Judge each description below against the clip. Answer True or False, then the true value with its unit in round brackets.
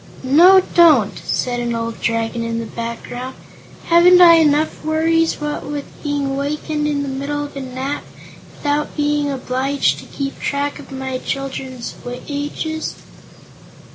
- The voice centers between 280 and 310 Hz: True (285 Hz)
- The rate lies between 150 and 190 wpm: False (140 wpm)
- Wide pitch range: False (2.6 semitones)